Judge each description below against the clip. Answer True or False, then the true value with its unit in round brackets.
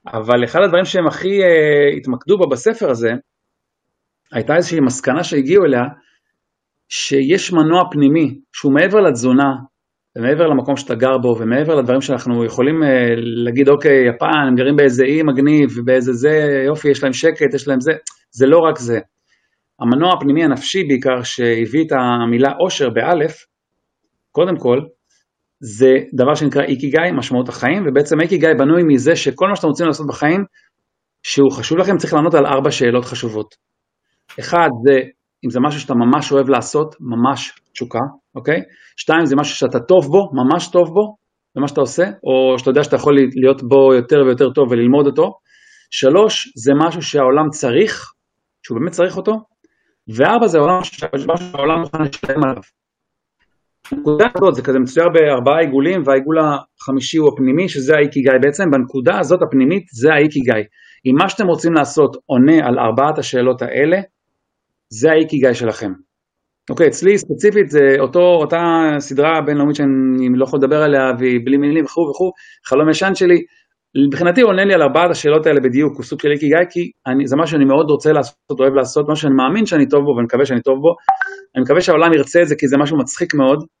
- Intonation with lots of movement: False (4.2 semitones)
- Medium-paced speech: False (165 wpm)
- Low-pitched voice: False (145 Hz)